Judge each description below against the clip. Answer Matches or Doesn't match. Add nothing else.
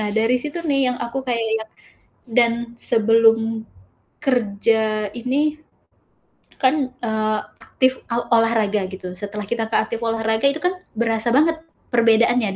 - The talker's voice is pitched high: Matches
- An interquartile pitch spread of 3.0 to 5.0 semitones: Doesn't match